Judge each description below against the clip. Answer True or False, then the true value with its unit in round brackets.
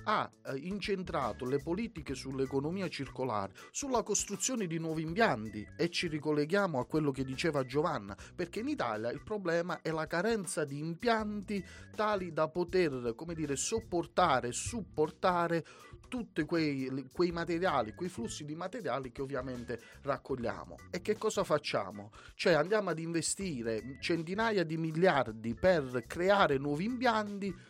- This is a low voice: False (165 Hz)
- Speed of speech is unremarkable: True (135 wpm)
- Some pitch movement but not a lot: False (6.0 semitones)